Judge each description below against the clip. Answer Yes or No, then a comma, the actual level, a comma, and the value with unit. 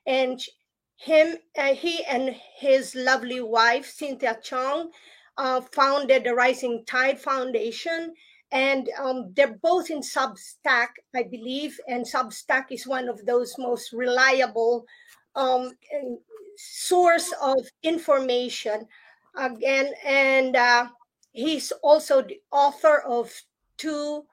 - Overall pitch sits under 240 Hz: No, very high, 265 Hz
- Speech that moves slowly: Yes, slow, 110 wpm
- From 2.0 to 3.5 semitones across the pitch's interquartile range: Yes, average, 3.0 semitones